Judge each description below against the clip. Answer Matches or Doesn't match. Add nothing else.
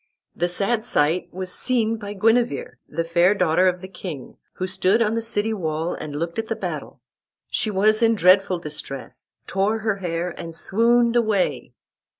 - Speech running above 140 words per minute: Matches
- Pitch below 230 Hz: Matches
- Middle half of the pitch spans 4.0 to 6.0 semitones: Matches